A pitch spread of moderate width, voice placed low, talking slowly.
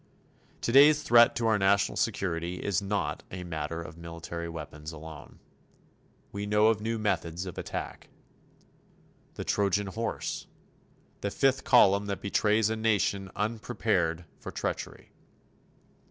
Yes: average, 4.6 semitones; low, 100 Hz; slow, 125 wpm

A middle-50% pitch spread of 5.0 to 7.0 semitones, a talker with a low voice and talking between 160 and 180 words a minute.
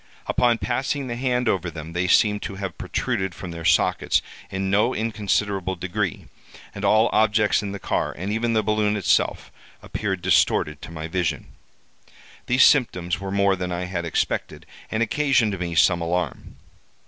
No: average, 3.5 semitones; low, 100 Hz; average, 165 wpm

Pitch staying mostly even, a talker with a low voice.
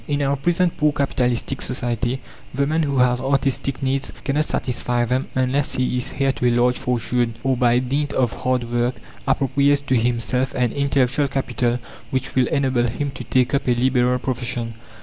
Yes: narrow, 2.0 semitones; low, 130 Hz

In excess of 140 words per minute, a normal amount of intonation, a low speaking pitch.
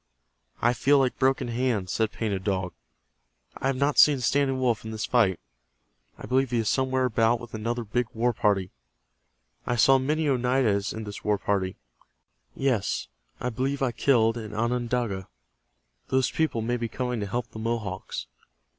Yes: average, 165 wpm; average, 3.2 semitones; low, 120 Hz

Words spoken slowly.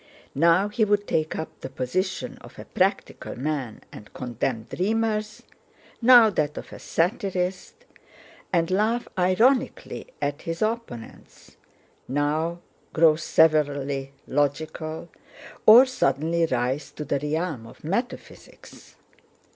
Yes: slow, 115 wpm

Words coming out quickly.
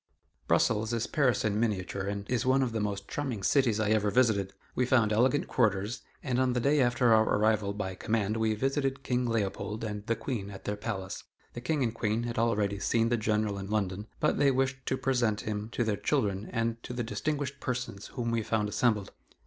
Yes: fast, 210 wpm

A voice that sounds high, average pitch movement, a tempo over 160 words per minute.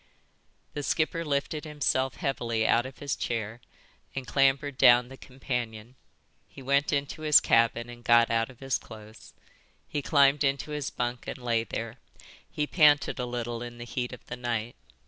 No: low, 125 Hz; average, 3.0 semitones; average, 170 wpm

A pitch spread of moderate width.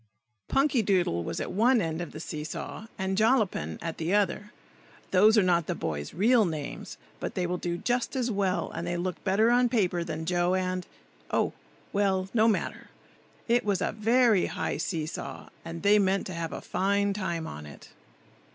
Yes: average, 4.1 semitones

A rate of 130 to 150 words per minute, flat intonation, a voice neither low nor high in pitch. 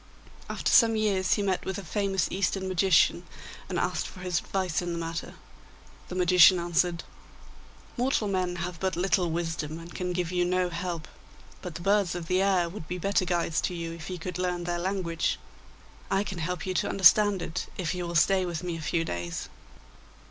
No: average, 200 wpm; narrow, 2.0 semitones; medium, 180 Hz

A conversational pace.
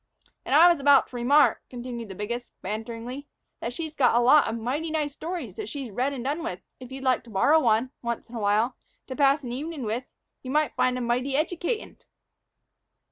No: fast, 210 wpm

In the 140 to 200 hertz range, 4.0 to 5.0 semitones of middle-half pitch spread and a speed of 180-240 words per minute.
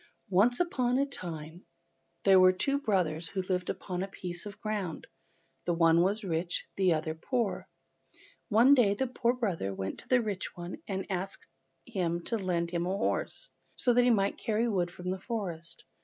Yes: high, 190 Hz; average, 4.6 semitones; average, 185 wpm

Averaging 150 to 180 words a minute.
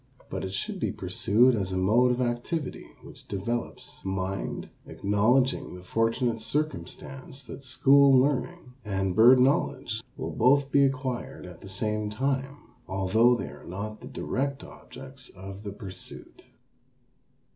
No: average, 140 wpm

